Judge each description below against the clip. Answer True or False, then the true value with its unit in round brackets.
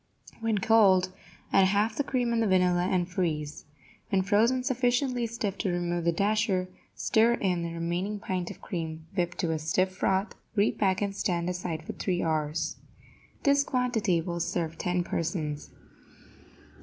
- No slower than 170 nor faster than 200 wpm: False (155 wpm)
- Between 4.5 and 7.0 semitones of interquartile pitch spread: False (4.1 semitones)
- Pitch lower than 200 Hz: True (185 Hz)